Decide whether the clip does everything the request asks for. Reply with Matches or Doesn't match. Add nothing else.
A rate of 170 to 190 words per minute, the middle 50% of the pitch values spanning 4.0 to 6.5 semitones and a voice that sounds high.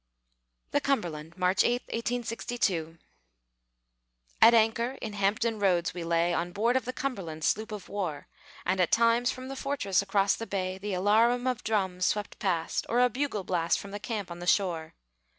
Matches